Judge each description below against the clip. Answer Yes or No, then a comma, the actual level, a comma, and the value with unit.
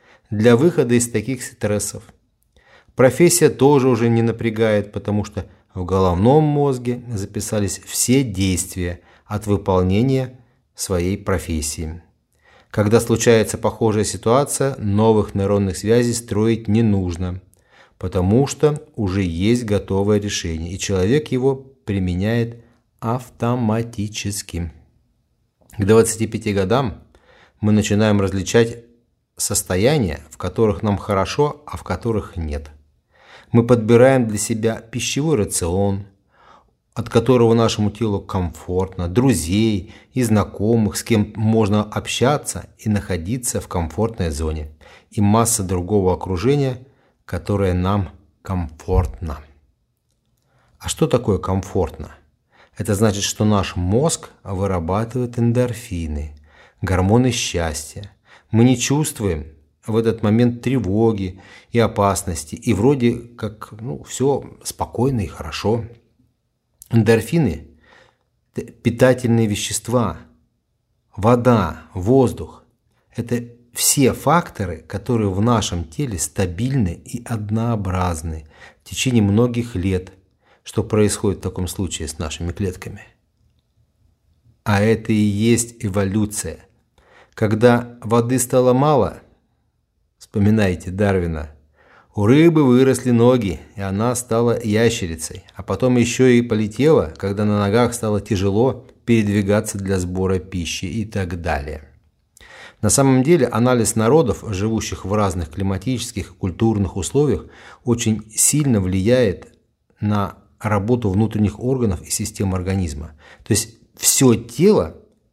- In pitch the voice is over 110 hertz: No, low, 105 Hz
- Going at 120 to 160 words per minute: No, slow, 110 wpm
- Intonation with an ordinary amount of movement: Yes, average, 3.8 semitones